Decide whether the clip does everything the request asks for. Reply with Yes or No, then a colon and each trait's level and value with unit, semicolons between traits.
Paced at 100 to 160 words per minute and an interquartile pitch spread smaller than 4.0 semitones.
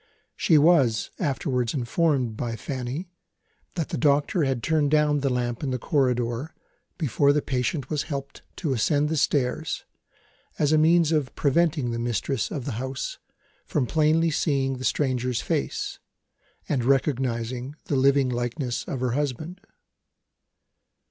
Yes: average, 140 wpm; average, 3.3 semitones